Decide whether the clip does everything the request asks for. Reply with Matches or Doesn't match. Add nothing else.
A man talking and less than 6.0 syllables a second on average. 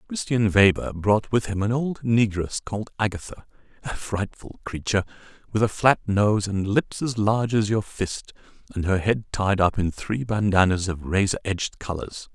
Matches